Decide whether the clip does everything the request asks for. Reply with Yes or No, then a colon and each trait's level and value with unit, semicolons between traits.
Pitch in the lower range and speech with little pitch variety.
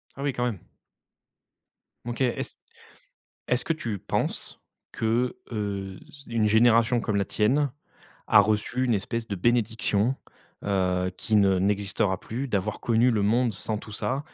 No: low, 110 Hz; average, 3.2 semitones